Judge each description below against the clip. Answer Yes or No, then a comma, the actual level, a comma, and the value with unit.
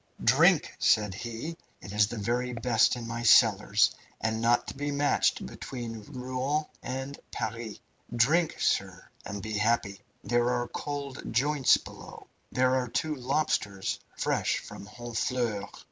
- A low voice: Yes, low, 120 Hz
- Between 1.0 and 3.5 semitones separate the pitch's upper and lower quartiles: Yes, average, 3.1 semitones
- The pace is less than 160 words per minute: Yes, average, 140 wpm